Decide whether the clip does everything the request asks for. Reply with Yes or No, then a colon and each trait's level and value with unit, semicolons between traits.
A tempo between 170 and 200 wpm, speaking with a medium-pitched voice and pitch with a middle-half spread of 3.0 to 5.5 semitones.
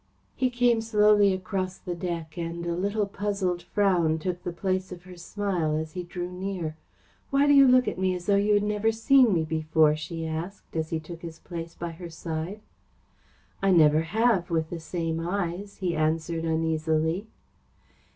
Yes: average, 180 wpm; medium, 175 Hz; average, 3.6 semitones